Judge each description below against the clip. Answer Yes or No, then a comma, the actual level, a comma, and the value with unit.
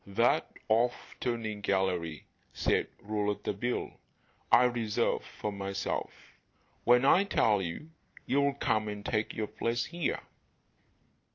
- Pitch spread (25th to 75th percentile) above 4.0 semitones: No, average, 3.3 semitones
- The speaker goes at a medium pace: No, slow, 110 wpm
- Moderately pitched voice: No, low, 110 Hz